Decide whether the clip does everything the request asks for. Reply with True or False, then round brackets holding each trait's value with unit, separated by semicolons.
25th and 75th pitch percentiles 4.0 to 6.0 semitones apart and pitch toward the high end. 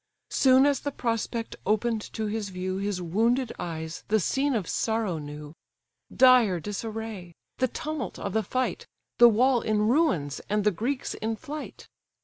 True (4.9 semitones; 220 Hz)